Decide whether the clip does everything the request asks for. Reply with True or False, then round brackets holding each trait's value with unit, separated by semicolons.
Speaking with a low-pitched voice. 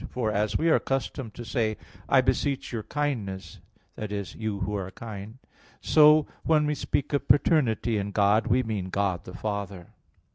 True (110 Hz)